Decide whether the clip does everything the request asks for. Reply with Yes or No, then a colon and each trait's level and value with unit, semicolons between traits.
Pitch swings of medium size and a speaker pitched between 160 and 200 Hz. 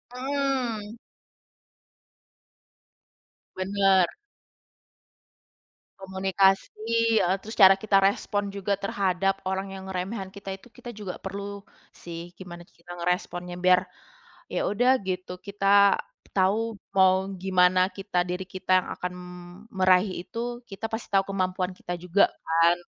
No: narrow, 1.8 semitones; high, 190 Hz